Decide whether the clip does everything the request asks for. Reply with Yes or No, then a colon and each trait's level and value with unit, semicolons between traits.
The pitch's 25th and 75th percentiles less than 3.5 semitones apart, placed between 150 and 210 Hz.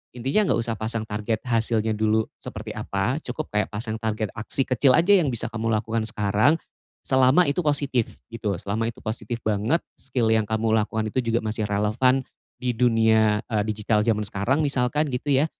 No: average, 2.9 semitones; low, 115 Hz